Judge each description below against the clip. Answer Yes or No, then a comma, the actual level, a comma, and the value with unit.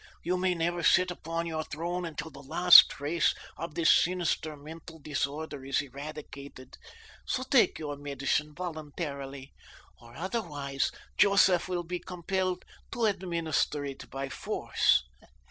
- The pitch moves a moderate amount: Yes, average, 3.8 semitones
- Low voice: No, medium, 160 Hz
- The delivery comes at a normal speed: No, slow, 130 wpm